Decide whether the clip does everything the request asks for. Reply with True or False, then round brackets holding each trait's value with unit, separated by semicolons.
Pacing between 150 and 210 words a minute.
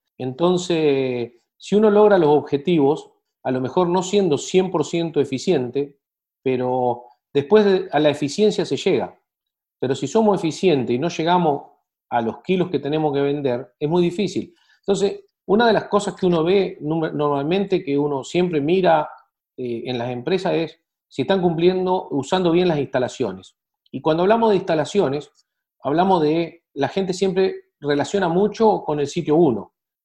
True (160 wpm)